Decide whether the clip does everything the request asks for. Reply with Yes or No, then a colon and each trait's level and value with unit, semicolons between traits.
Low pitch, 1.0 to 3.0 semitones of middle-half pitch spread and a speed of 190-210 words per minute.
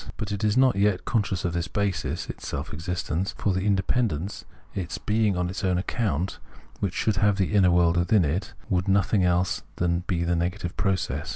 Yes: very low, 95 Hz; average, 2.7 semitones; fast, 205 wpm